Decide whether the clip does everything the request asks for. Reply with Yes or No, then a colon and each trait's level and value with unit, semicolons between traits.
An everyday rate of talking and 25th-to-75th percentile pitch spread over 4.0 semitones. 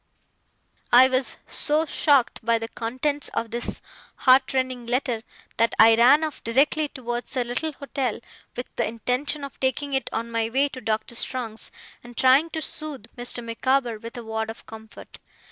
No: average, 170 wpm; average, 3.1 semitones